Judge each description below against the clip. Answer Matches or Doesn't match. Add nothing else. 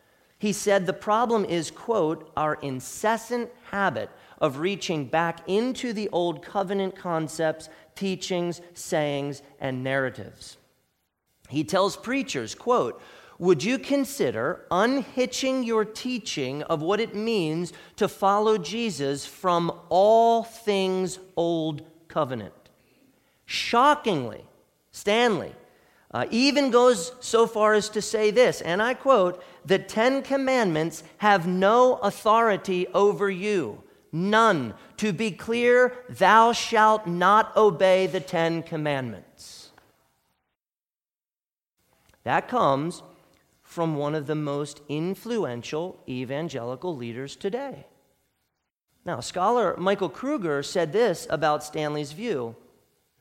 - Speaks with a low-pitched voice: Doesn't match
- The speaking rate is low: Matches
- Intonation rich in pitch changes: Matches